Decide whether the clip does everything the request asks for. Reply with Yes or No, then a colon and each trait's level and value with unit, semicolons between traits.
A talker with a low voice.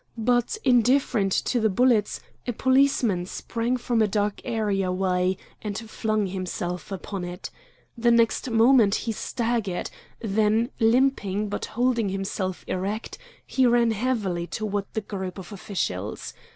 No: high, 215 Hz